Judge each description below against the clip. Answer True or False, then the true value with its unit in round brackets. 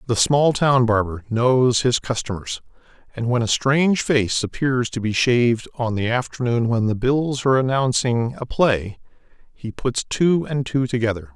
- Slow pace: False (170 wpm)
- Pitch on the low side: True (120 Hz)